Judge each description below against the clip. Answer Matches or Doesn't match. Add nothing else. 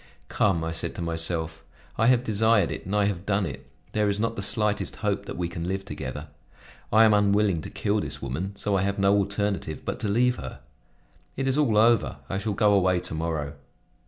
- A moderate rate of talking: Doesn't match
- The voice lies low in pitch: Matches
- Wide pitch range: Doesn't match